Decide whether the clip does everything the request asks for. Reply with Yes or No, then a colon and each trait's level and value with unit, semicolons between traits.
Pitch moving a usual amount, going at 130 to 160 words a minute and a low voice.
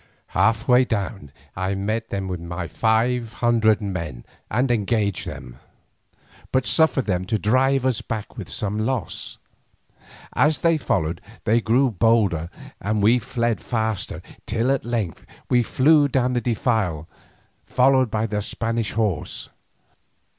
Yes: average, 3.7 semitones; average, 140 wpm; low, 115 Hz